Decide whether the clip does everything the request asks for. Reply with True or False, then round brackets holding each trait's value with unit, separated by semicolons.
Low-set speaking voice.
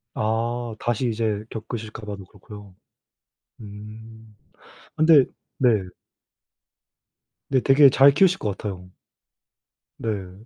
True (110 Hz)